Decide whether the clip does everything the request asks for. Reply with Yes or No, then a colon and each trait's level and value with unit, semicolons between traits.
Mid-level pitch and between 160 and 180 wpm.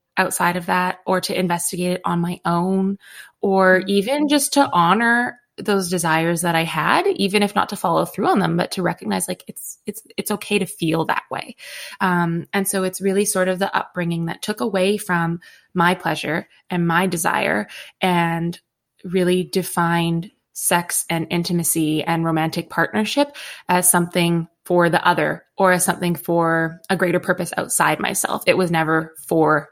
Yes: medium, 180 Hz; average, 170 wpm